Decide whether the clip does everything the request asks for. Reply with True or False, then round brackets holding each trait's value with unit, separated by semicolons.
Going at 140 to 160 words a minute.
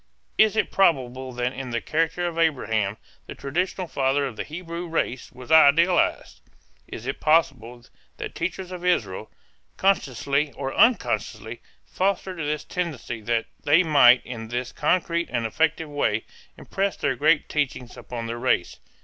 True (150 wpm)